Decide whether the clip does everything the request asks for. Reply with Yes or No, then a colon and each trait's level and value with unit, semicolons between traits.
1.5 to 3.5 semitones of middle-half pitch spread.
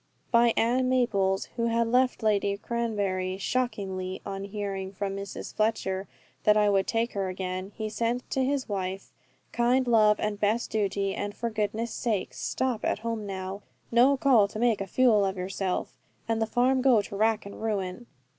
Yes: average, 3.1 semitones